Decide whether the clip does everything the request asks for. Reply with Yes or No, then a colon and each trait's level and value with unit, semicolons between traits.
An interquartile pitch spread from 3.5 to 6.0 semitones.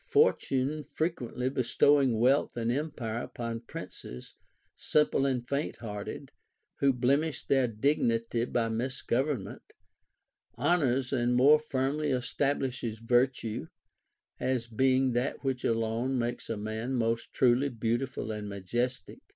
No: average, 2.9 semitones